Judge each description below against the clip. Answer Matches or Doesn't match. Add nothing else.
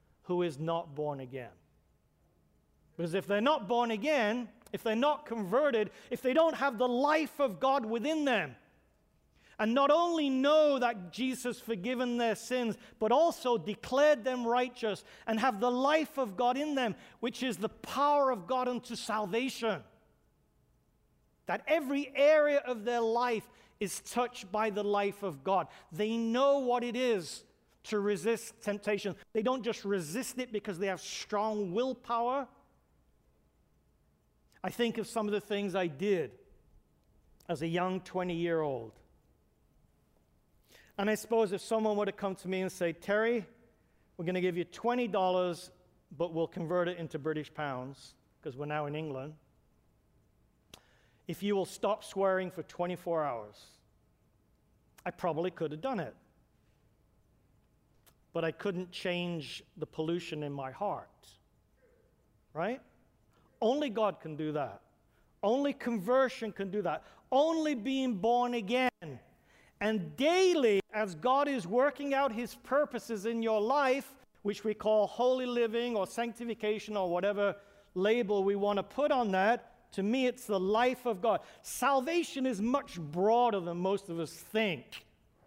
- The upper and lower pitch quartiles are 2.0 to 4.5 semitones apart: Doesn't match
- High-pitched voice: Matches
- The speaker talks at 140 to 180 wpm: Matches